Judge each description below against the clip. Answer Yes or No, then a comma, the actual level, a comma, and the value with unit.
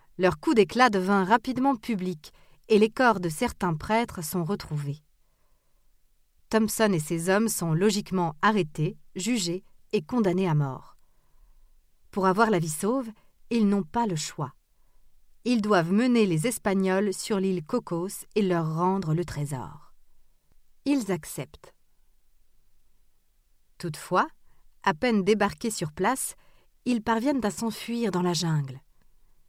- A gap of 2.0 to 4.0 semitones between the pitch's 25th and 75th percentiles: No, average, 4.6 semitones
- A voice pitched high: Yes, high, 195 Hz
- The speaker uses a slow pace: Yes, slow, 130 wpm